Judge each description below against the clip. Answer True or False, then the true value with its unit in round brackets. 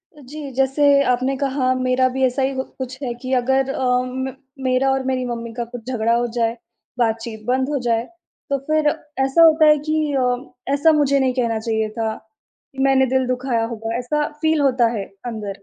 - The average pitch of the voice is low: False (255 Hz)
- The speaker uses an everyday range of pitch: False (2.3 semitones)